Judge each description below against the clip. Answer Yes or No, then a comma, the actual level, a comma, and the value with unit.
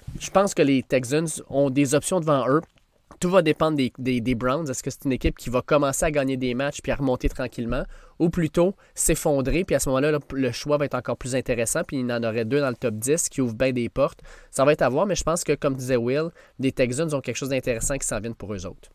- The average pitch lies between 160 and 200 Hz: No, low, 135 Hz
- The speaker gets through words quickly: Yes, fast, 270 wpm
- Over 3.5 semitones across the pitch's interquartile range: No, average, 3.1 semitones